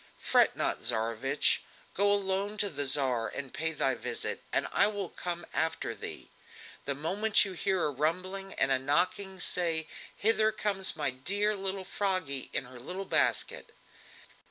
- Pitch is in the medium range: Yes, medium, 175 Hz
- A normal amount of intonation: No, wide, 6.0 semitones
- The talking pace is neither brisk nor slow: Yes, average, 155 wpm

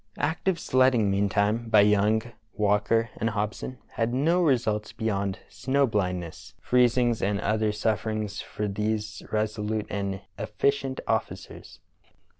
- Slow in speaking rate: Yes, slow, 125 wpm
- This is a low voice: Yes, low, 110 Hz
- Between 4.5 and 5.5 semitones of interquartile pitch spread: No, average, 2.7 semitones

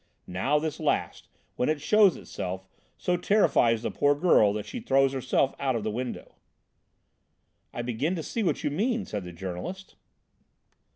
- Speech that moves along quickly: No, average, 165 wpm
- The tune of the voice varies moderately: No, wide, 8.4 semitones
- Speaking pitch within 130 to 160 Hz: Yes, low, 135 Hz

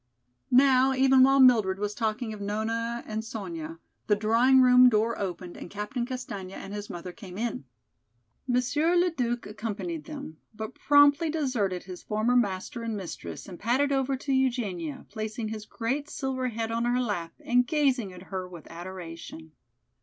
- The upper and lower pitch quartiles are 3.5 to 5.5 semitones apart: Yes, average, 4.6 semitones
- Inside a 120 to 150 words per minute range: No, average, 165 wpm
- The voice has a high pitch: Yes, high, 230 Hz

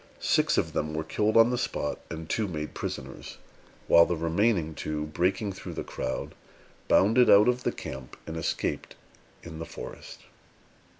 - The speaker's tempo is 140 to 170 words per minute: Yes, average, 165 wpm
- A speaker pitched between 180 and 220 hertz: No, very low, 85 Hz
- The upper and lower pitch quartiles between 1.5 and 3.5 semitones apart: No, average, 5.2 semitones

